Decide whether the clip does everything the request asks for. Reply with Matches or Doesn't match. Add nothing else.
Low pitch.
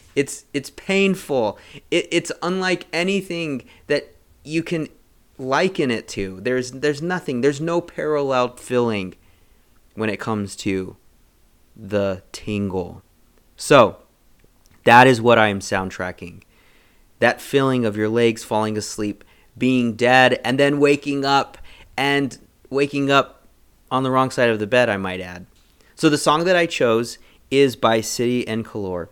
Matches